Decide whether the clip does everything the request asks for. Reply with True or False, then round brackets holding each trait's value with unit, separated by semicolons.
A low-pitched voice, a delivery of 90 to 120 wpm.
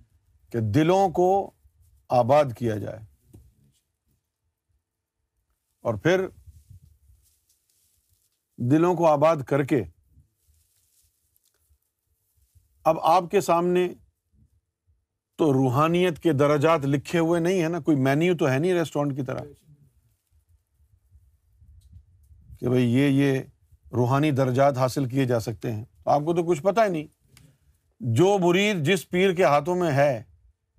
True (120 Hz; 115 wpm)